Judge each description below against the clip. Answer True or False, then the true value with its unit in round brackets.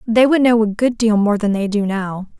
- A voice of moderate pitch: False (215 Hz)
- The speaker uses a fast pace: True (275 wpm)